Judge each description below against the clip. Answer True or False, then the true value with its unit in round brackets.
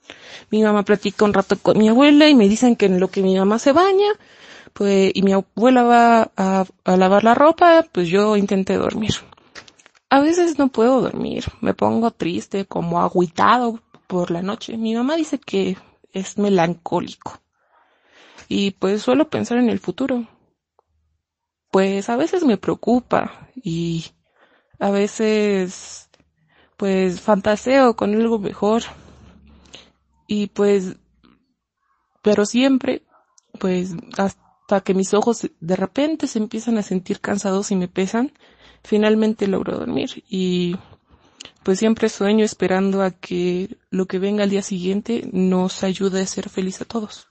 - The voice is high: True (205 Hz)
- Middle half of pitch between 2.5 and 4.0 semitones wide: True (3.4 semitones)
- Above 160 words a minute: False (145 wpm)